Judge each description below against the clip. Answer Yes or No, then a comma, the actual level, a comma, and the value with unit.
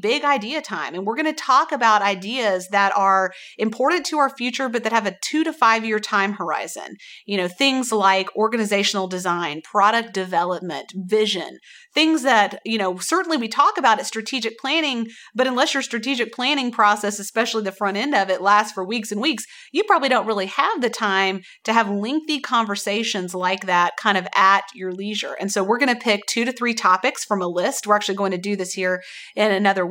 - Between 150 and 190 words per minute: No, fast, 205 wpm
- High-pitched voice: Yes, high, 215 Hz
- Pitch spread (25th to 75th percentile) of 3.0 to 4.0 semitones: No, average, 4.7 semitones